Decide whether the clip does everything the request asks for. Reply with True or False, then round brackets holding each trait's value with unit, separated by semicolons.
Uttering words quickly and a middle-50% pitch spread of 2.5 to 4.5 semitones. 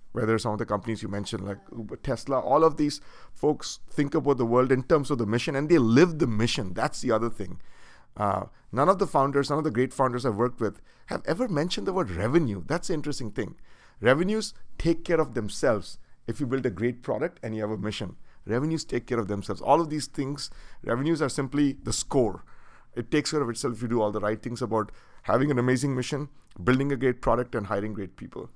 False (230 wpm; 4.9 semitones)